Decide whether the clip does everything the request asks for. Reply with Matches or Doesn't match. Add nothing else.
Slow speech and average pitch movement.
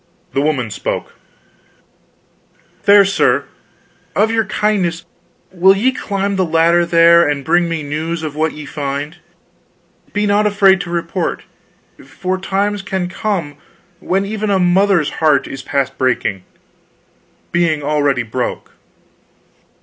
Matches